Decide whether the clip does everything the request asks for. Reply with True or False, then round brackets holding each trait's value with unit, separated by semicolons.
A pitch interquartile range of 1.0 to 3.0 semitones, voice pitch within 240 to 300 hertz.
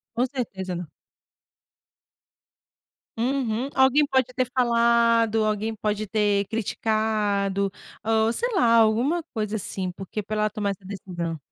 False (2.7 semitones; 220 Hz)